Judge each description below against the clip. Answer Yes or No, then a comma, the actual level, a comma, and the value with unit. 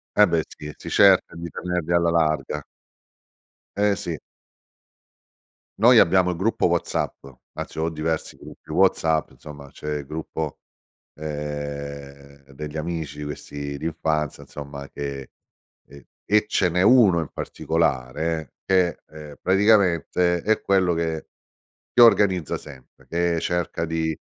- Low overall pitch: Yes, very low, 80 Hz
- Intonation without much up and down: No, average, 3.3 semitones